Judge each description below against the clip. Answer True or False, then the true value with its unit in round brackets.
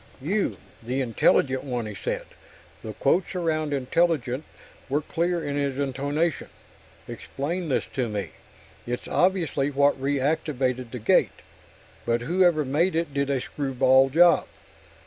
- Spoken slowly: True (130 wpm)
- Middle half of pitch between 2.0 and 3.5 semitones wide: False (3.9 semitones)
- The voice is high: False (140 Hz)